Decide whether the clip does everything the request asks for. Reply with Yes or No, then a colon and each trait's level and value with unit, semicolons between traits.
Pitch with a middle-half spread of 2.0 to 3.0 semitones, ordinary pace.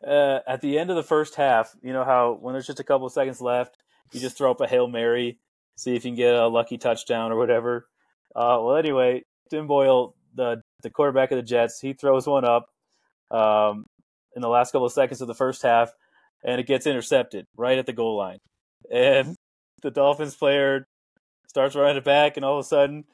No: average, 2.7 semitones; fast, 220 wpm